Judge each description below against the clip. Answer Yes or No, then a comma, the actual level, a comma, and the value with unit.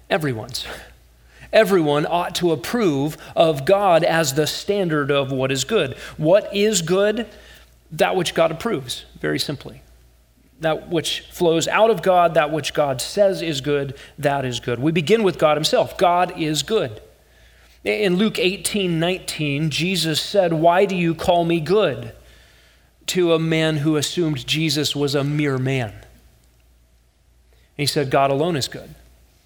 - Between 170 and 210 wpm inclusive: No, average, 150 wpm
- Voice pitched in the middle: Yes, medium, 155 Hz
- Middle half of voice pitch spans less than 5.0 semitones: No, wide, 5.4 semitones